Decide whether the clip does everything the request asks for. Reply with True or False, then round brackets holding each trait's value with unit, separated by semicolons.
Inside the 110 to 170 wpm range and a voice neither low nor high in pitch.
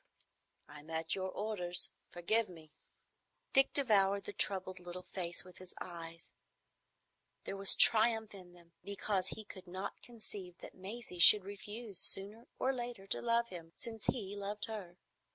False (150 wpm; 195 Hz)